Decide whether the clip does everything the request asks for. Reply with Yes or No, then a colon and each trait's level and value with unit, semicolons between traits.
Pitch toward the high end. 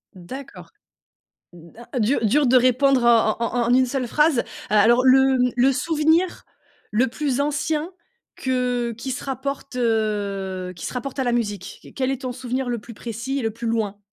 Yes: very high, 250 Hz